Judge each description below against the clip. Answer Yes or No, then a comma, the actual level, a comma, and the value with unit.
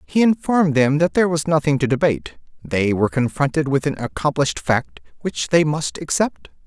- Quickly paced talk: No, average, 180 wpm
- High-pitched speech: No, medium, 140 Hz